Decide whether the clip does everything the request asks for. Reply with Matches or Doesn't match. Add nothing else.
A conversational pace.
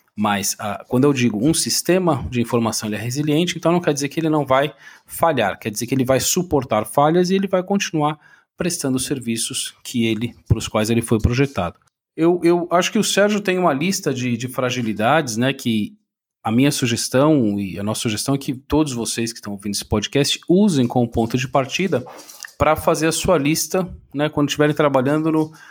Doesn't match